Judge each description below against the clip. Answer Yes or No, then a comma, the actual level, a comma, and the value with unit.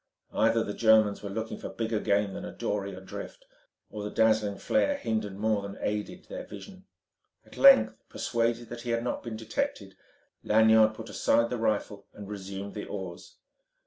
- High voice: No, low, 110 Hz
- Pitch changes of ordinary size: No, narrow, 2.0 semitones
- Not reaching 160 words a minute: No, average, 175 wpm